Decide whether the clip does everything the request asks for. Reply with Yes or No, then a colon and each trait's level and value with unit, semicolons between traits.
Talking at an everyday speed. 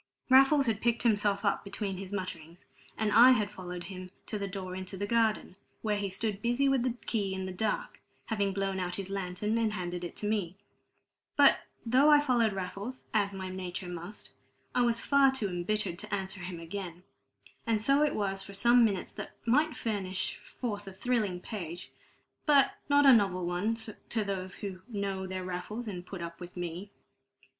Yes: average, 190 wpm